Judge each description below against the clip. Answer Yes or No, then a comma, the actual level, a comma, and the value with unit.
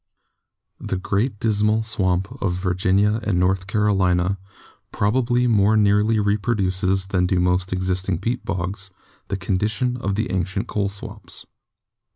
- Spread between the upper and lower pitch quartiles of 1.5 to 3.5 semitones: Yes, narrow, 2.4 semitones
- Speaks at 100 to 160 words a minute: Yes, average, 140 wpm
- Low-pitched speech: Yes, low, 100 Hz